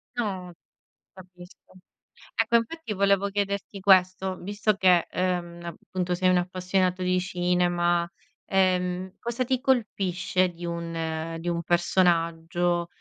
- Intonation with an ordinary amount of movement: No, narrow, 1.9 semitones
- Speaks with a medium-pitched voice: Yes, medium, 180 Hz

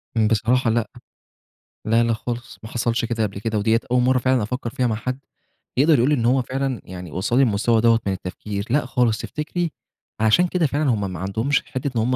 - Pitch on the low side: Yes, low, 115 Hz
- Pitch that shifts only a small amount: No, average, 3.0 semitones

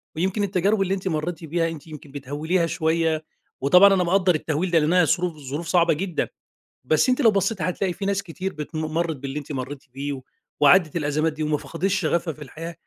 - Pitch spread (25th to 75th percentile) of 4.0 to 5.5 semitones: No, average, 3.4 semitones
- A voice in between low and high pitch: Yes, medium, 165 Hz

